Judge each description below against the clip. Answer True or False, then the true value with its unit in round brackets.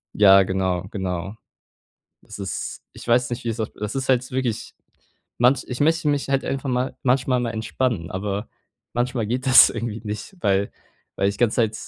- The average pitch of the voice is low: True (115 Hz)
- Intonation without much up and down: False (4.2 semitones)